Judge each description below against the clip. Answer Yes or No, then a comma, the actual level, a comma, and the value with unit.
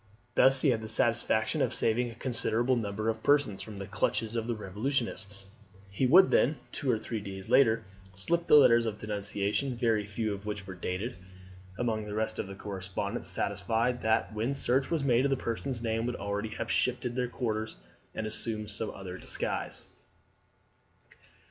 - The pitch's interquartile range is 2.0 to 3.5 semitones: Yes, average, 3.0 semitones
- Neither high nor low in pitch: No, low, 110 Hz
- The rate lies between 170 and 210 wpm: Yes, average, 175 wpm